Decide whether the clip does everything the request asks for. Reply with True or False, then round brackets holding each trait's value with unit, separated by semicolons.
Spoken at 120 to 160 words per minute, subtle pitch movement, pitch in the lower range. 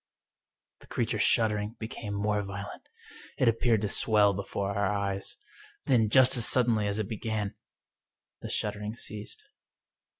True (140 wpm; 1.7 semitones; 105 Hz)